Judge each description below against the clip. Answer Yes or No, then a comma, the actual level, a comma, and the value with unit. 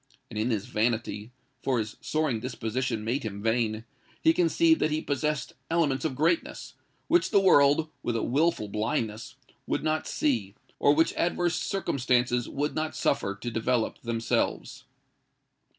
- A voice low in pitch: Yes, low, 125 Hz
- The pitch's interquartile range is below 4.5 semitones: No, wide, 5.5 semitones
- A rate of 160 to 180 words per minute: No, average, 140 wpm